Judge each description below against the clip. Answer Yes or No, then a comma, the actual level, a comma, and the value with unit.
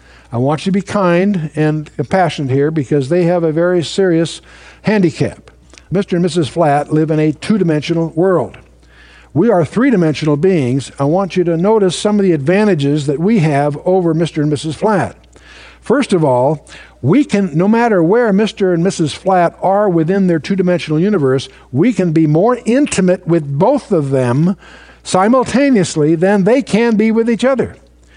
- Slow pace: No, average, 175 wpm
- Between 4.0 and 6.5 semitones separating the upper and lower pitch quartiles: Yes, average, 4.7 semitones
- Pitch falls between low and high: Yes, medium, 175 Hz